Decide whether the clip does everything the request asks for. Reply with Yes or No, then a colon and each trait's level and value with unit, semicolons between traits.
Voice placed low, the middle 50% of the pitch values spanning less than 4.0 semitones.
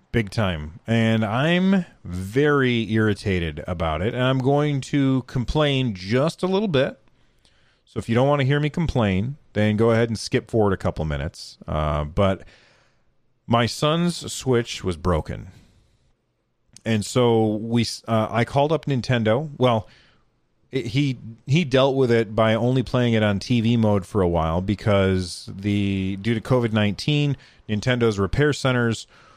No: low, 115 Hz; average, 4.3 semitones